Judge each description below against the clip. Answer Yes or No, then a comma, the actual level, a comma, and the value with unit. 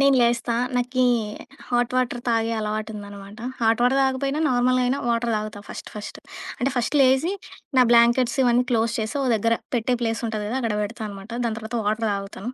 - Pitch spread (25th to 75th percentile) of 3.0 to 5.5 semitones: No, narrow, 2.5 semitones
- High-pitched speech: Yes, high, 235 Hz